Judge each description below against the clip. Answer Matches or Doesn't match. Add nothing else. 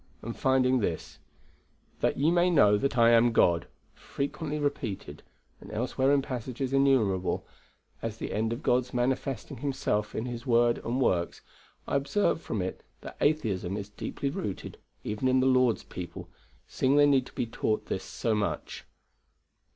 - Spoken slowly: Doesn't match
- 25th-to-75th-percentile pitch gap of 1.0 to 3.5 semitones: Doesn't match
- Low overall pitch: Matches